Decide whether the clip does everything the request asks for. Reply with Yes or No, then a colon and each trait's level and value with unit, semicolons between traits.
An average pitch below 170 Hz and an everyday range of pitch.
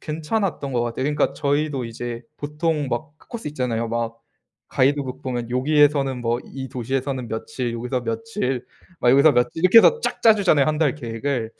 Yes: low, 135 Hz; average, 3.8 semitones